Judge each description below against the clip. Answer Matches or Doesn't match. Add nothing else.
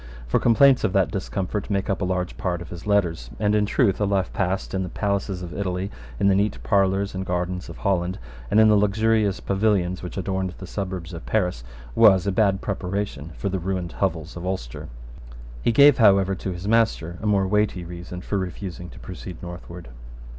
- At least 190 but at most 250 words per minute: Matches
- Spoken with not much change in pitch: Matches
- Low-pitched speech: Matches